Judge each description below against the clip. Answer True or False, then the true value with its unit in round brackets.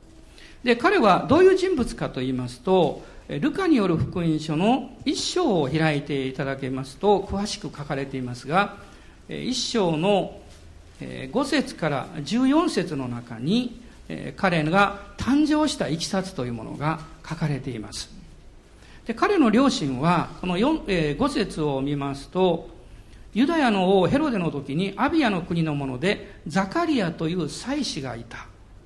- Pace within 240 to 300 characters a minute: True (270 characters per minute)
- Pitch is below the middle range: False (175 Hz)